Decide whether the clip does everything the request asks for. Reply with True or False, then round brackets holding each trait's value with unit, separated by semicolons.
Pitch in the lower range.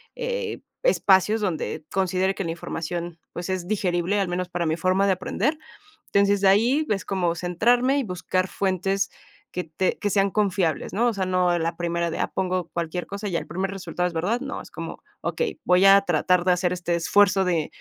False (185 Hz)